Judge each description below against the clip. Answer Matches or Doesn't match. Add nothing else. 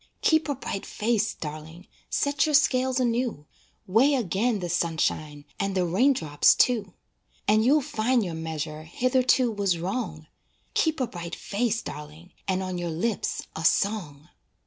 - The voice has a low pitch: Doesn't match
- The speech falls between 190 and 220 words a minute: Doesn't match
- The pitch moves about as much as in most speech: Doesn't match